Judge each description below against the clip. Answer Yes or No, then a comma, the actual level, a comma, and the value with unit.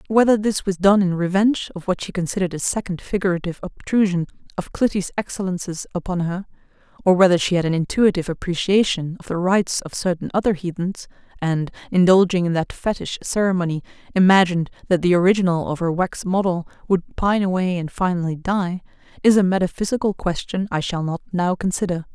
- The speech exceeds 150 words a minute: Yes, average, 170 wpm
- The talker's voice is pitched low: No, medium, 185 Hz